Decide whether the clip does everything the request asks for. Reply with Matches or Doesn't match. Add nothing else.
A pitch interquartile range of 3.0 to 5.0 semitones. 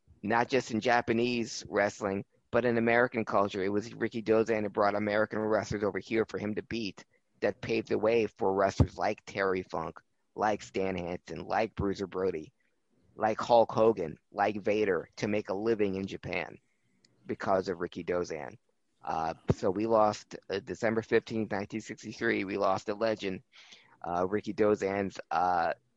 Doesn't match